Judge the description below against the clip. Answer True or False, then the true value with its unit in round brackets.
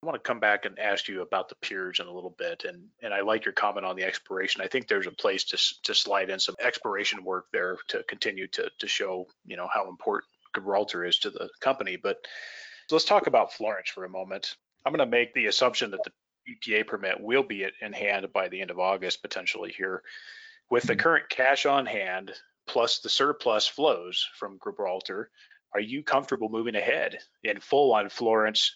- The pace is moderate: False (210 wpm)